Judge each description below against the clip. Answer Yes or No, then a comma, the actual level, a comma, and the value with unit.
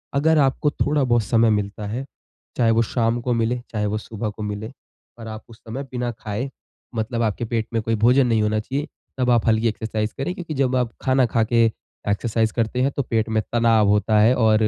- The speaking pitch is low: Yes, low, 115 Hz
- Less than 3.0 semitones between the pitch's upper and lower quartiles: Yes, narrow, 2.4 semitones